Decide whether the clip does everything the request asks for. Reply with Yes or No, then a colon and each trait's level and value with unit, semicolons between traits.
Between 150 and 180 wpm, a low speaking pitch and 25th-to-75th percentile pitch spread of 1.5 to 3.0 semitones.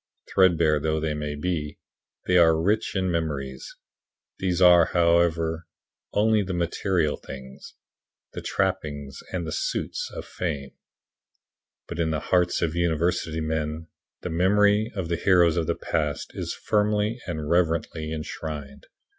No: average, 140 wpm; very low, 85 Hz; average, 2.7 semitones